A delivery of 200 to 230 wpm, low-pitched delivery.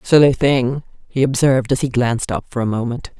Yes: fast, 205 wpm; low, 125 Hz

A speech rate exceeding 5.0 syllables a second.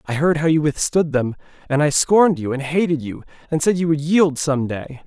Yes: 5.3 syllables/s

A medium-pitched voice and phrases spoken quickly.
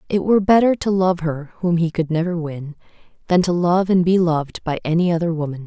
Yes: medium, 170 Hz; fast, 225 wpm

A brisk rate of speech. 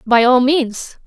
No: average, 170 wpm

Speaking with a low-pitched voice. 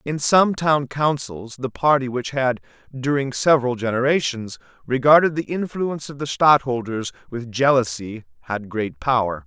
Yes: low, 130 Hz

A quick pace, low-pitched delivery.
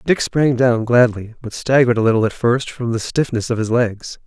Yes: fast, 225 wpm; low, 120 Hz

